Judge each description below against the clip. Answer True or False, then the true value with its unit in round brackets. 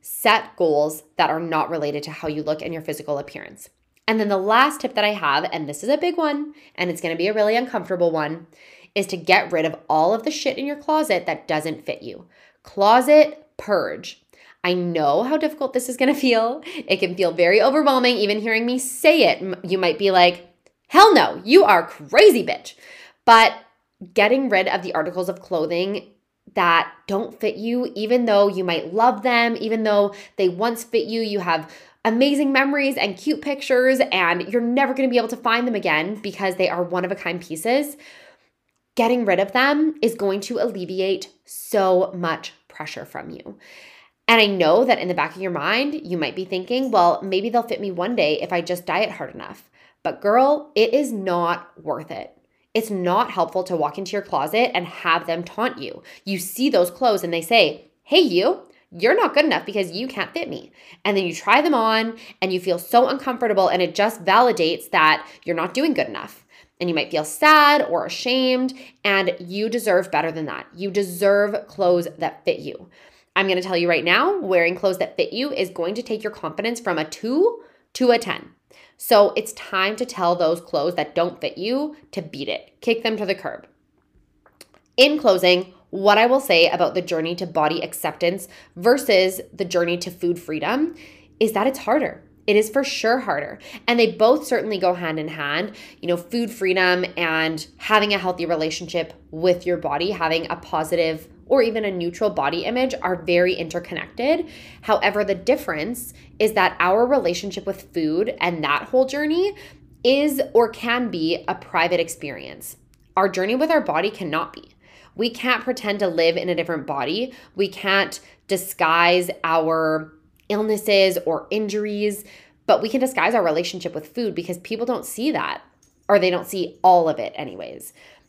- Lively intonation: True (5.9 semitones)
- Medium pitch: False (200 Hz)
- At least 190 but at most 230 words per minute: True (195 wpm)